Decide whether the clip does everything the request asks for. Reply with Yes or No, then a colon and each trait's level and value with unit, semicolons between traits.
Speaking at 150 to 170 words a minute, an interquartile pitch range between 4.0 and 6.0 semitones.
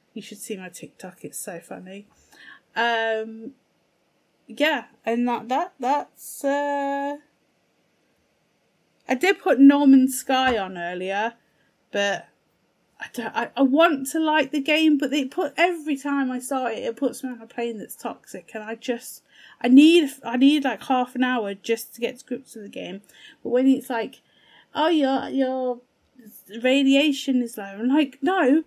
No: average, 165 wpm; average, 3.6 semitones